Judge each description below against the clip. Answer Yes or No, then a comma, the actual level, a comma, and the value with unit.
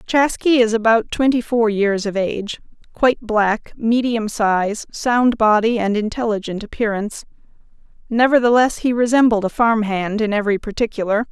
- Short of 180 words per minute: Yes, average, 140 wpm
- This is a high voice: Yes, high, 225 Hz